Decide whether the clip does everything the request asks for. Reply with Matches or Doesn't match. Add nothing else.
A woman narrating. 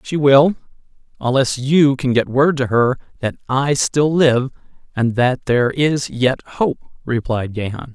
Doesn't match